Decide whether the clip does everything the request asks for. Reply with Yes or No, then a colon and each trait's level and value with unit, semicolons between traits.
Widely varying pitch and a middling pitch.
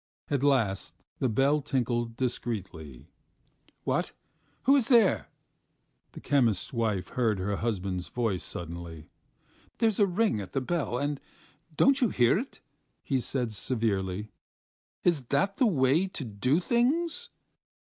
No: wide, 8.8 semitones; low, 125 Hz